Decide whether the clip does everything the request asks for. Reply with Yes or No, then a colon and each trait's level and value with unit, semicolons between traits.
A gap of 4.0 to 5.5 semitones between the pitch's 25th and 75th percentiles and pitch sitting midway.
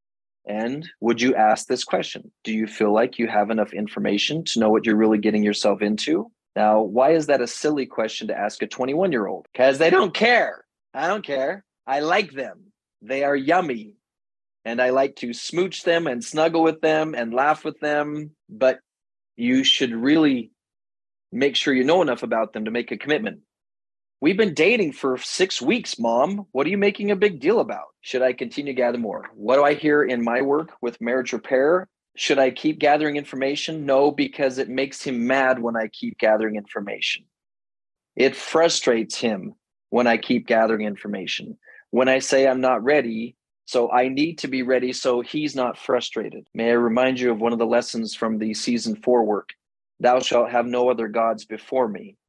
No: average, 4.6 semitones; low, 125 Hz